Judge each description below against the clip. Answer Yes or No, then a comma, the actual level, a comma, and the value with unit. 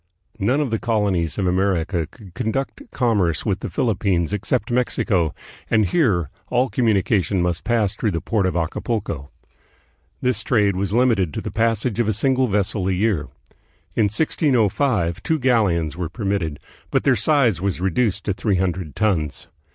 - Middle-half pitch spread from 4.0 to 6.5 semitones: Yes, average, 4.5 semitones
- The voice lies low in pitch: Yes, low, 100 Hz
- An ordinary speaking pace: Yes, average, 165 wpm